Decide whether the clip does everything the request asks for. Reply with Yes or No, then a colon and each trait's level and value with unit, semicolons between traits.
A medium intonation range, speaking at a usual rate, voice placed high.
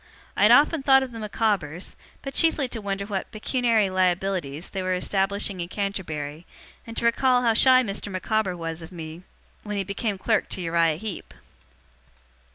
Yes: average, 4.3 semitones; average, 170 wpm; high, 200 Hz